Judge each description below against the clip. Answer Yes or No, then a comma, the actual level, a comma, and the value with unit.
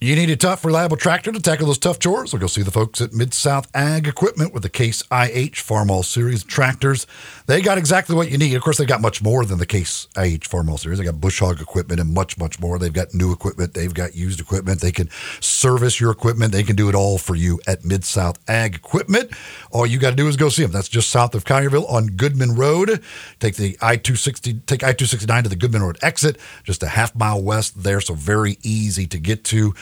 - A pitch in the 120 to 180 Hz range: No, low, 110 Hz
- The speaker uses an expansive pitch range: Yes, wide, 6.2 semitones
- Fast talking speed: Yes, fast, 250 wpm